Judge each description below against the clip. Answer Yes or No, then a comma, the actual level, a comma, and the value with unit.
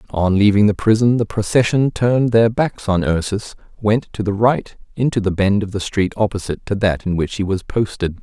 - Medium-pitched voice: No, low, 105 Hz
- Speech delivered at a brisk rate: Yes, fast, 210 wpm